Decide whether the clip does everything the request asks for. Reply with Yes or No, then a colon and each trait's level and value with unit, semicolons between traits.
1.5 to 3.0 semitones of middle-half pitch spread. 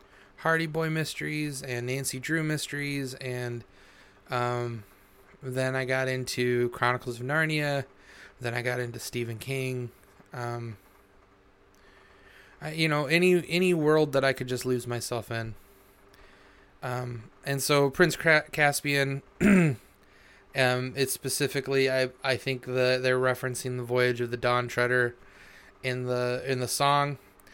Yes: average, 2.7 semitones